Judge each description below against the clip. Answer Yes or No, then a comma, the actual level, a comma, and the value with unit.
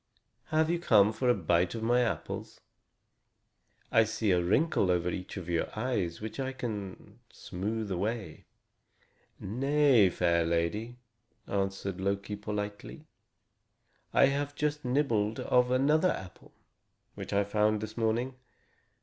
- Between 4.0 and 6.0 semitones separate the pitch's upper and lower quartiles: Yes, average, 4.6 semitones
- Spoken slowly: Yes, slow, 130 wpm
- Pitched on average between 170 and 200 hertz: No, low, 110 Hz